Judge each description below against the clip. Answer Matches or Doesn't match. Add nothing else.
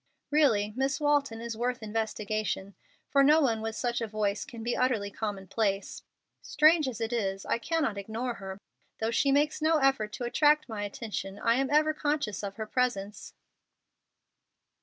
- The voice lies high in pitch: Matches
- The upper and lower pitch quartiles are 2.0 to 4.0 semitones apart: Doesn't match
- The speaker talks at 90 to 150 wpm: Doesn't match